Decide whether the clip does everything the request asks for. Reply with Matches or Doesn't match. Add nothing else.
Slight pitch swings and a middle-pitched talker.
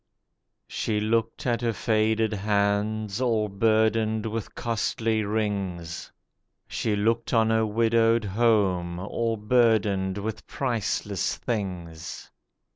Doesn't match